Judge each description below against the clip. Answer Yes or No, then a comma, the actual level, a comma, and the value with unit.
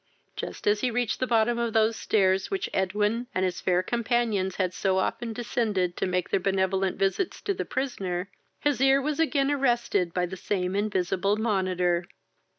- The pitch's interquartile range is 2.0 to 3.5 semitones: No, average, 4.2 semitones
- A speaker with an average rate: Yes, average, 175 wpm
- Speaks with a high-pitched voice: Yes, high, 205 Hz